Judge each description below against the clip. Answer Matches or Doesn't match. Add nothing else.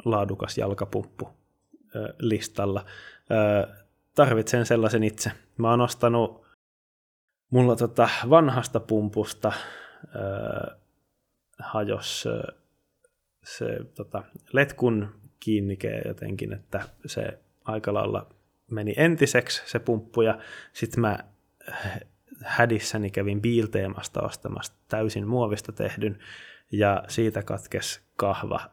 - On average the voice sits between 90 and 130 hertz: Matches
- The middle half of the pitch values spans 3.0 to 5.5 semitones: Doesn't match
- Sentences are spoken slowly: Matches